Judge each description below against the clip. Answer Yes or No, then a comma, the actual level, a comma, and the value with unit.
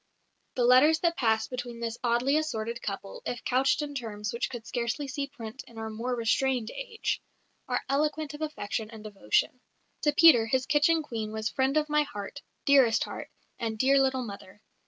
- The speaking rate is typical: Yes, average, 180 wpm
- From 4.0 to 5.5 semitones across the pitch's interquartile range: Yes, average, 4.4 semitones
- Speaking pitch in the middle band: No, very high, 250 Hz